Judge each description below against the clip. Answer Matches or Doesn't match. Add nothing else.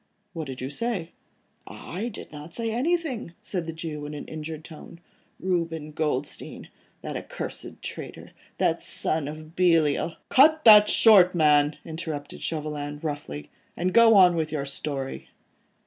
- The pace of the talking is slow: Doesn't match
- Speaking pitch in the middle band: Matches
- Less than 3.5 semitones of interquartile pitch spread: Doesn't match